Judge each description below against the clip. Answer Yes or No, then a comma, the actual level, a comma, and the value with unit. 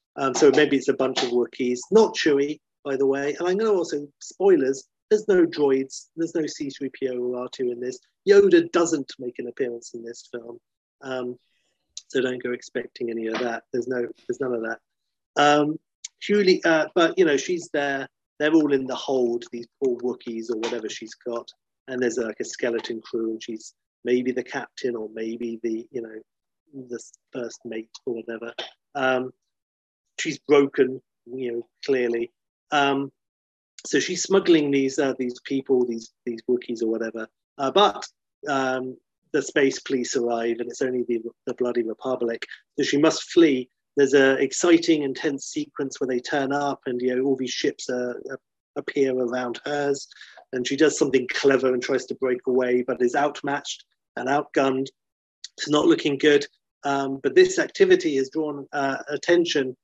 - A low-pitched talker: Yes, low, 130 Hz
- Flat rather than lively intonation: No, average, 3.2 semitones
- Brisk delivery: No, average, 175 wpm